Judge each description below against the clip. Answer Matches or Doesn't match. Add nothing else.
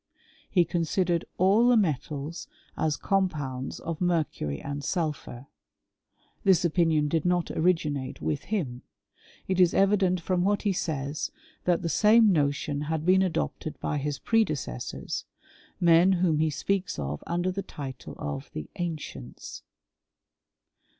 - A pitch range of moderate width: Matches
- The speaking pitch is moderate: Matches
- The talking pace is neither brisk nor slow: Doesn't match